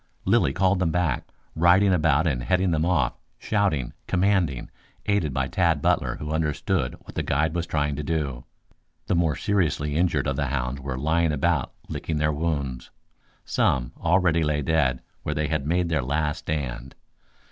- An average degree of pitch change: Yes, average, 3.5 semitones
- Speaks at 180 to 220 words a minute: No, average, 170 wpm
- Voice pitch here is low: Yes, very low, 75 Hz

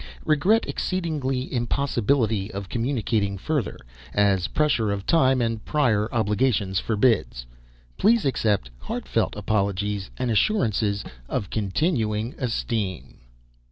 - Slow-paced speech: Yes, slow, 100 wpm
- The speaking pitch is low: Yes, low, 115 Hz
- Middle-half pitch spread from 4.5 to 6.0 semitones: Yes, average, 4.8 semitones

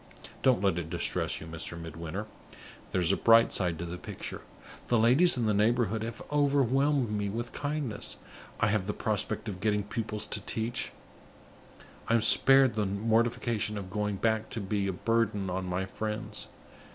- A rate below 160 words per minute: No, average, 170 wpm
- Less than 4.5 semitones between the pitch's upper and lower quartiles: Yes, average, 3.2 semitones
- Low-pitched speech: Yes, low, 105 Hz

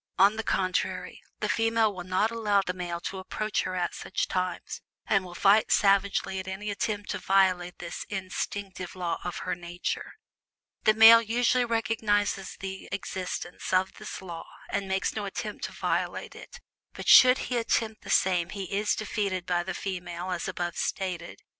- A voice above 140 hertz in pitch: Yes, high, 190 Hz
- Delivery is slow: No, average, 170 wpm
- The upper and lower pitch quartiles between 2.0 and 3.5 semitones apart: Yes, narrow, 2.5 semitones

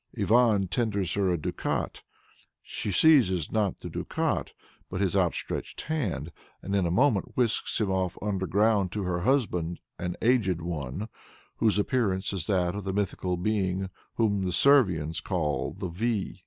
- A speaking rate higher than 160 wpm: No, average, 155 wpm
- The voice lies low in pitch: Yes, very low, 95 Hz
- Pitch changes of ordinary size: Yes, average, 3.4 semitones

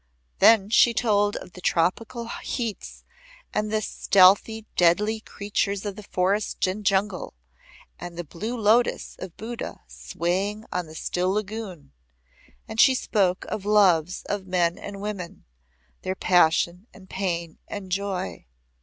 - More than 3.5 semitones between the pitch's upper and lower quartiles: No, average, 2.9 semitones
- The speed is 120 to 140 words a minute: Yes, slow, 135 wpm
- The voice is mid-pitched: No, high, 200 Hz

